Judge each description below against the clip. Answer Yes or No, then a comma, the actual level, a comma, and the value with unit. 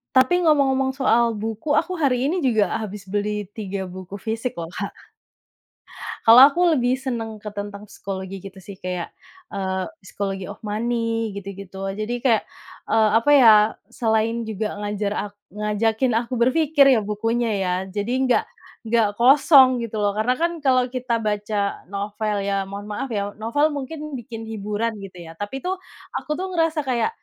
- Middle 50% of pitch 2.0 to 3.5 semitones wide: No, average, 4.1 semitones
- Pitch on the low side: No, high, 220 Hz